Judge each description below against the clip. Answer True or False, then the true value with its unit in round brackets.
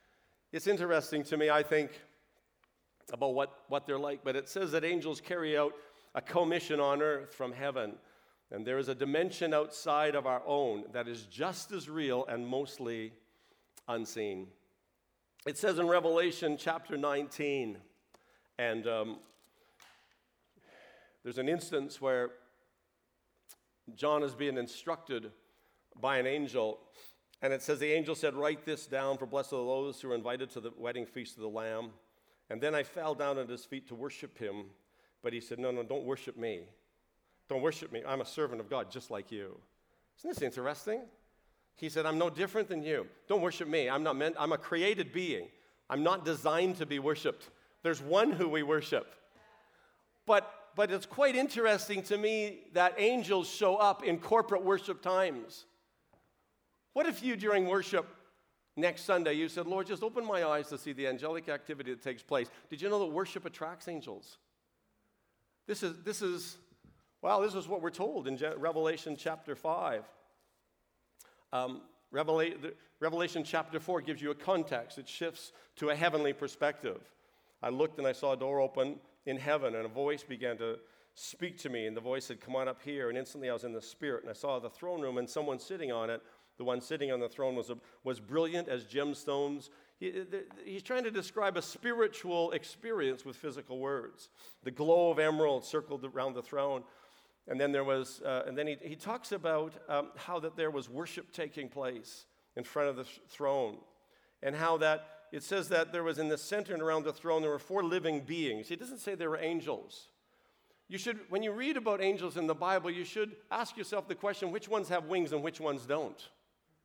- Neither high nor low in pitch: True (155 Hz)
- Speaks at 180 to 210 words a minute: True (190 wpm)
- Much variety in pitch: False (5.0 semitones)